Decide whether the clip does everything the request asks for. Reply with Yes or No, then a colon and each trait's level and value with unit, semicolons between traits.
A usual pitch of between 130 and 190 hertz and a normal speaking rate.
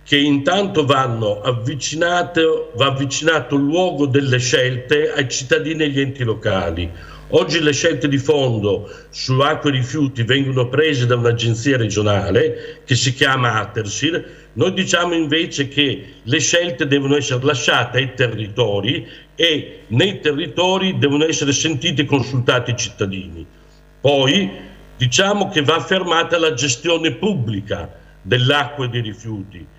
Yes: medium, 140 Hz; average, 135 wpm